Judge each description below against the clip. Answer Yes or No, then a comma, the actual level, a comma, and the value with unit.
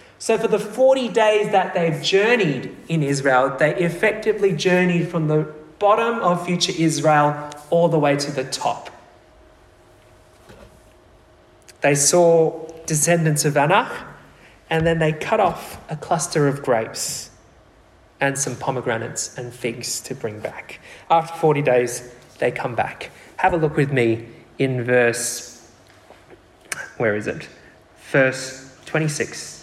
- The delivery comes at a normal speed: No, slow, 130 wpm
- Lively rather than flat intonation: No, average, 5.0 semitones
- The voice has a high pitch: No, medium, 150 Hz